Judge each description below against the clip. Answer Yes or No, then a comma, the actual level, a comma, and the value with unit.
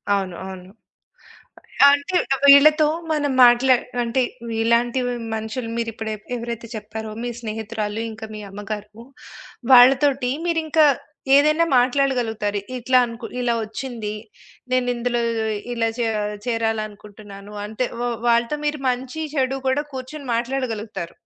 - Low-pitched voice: No, high, 235 Hz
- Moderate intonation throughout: Yes, average, 3.3 semitones